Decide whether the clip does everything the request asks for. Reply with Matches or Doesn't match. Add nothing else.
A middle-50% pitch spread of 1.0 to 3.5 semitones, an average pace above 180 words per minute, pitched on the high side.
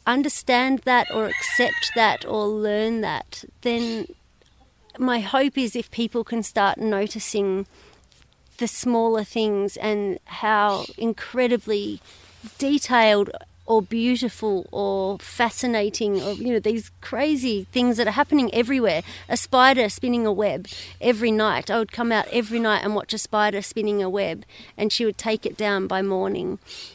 Doesn't match